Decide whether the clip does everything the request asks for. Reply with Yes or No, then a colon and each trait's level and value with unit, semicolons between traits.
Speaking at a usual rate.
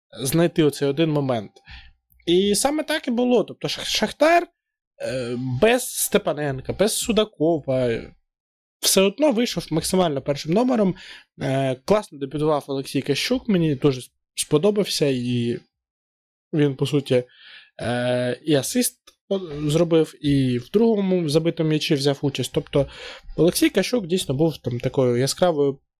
Yes: average, 115 wpm